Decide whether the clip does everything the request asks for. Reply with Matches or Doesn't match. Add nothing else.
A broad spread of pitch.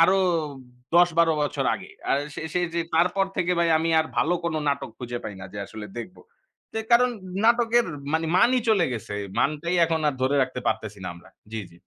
Matches